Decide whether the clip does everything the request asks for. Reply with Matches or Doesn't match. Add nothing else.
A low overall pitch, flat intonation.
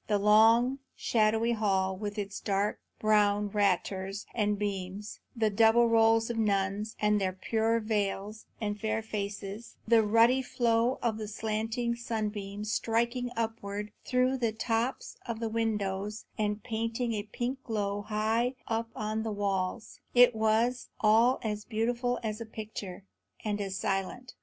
Doesn't match